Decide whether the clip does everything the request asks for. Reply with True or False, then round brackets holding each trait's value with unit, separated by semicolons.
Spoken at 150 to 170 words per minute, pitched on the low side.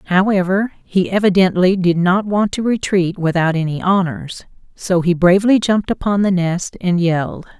False (160 wpm; 185 Hz)